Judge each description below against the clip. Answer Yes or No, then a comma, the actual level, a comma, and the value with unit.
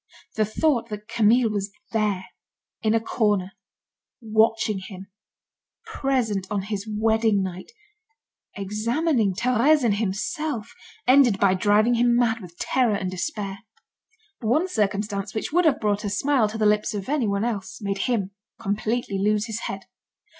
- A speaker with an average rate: Yes, average, 145 wpm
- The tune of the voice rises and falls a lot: No, average, 3.0 semitones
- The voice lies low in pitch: No, high, 215 Hz